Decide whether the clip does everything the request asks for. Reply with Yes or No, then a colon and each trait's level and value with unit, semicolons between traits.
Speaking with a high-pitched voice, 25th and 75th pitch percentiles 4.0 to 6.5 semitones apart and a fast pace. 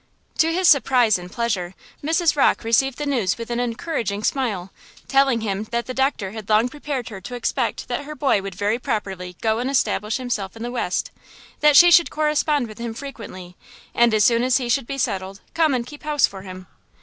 Yes: high, 235 Hz; average, 5.0 semitones; fast, 210 wpm